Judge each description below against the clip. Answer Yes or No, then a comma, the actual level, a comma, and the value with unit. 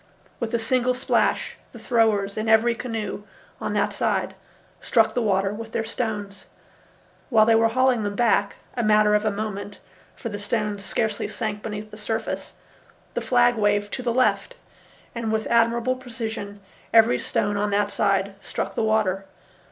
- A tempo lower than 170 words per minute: Yes, average, 160 wpm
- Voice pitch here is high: Yes, high, 220 Hz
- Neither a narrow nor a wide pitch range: No, narrow, 2.2 semitones